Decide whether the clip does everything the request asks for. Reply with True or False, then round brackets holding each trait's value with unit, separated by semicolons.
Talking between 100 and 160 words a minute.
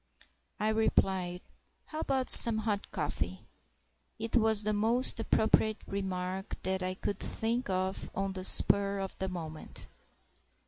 True (135 wpm)